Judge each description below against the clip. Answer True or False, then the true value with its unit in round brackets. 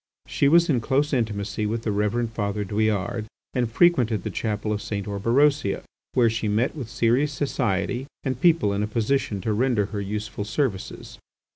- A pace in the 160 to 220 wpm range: True (170 wpm)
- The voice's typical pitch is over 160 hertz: False (110 Hz)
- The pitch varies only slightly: False (3.9 semitones)